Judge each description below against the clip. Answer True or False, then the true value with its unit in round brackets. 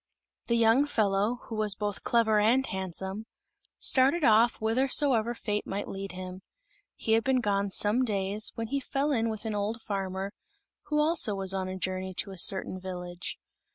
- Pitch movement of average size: True (3.4 semitones)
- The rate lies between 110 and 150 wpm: False (175 wpm)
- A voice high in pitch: True (210 Hz)